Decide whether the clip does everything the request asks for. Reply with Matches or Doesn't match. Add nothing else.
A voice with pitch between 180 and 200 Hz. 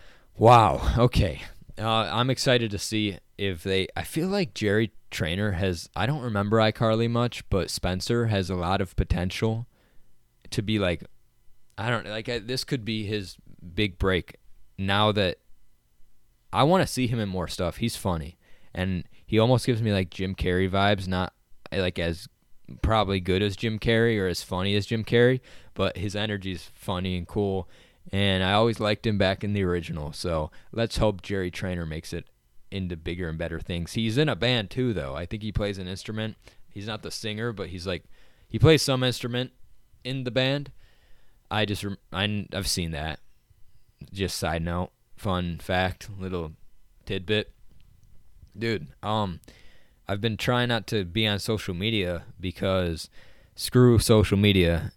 Doesn't match